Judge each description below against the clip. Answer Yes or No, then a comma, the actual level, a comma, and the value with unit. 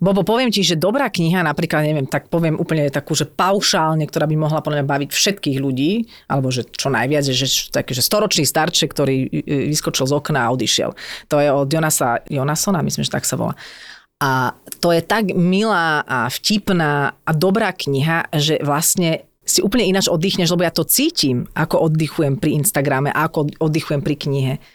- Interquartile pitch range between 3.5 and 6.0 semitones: Yes, average, 3.8 semitones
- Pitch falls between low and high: Yes, medium, 155 Hz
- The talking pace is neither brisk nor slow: No, fast, 180 wpm